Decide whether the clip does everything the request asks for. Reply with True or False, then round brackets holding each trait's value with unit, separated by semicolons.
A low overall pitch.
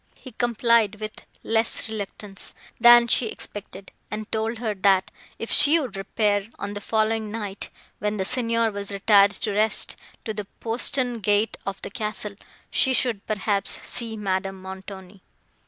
False (215 Hz)